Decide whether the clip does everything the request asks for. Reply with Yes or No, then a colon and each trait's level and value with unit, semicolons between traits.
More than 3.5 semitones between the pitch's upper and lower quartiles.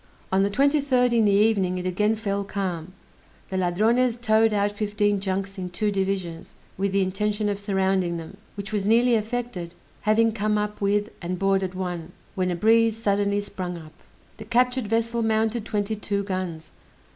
No: average, 2.7 semitones